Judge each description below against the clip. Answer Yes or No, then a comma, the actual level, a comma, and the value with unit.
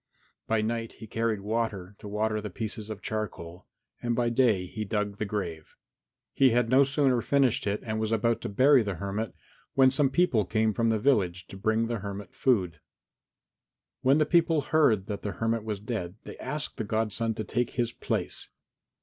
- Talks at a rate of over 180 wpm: Yes, average, 190 wpm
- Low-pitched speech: Yes, low, 110 Hz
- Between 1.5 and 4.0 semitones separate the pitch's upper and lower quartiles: Yes, average, 2.9 semitones